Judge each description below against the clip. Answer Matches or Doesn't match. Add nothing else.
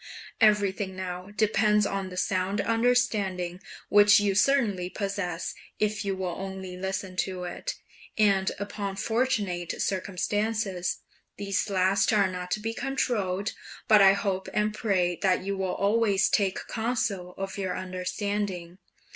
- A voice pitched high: Matches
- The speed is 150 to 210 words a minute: Doesn't match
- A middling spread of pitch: Doesn't match